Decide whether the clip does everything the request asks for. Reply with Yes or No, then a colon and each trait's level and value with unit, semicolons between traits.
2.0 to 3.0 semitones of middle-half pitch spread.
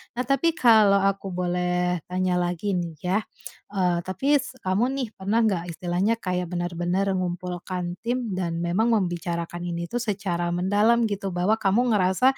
No: average, 3.5 semitones